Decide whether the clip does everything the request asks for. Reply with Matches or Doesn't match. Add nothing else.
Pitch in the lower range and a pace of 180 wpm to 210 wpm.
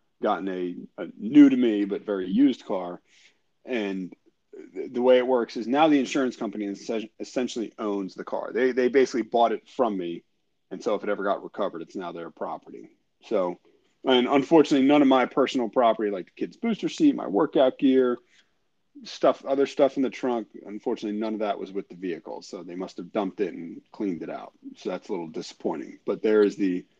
Matches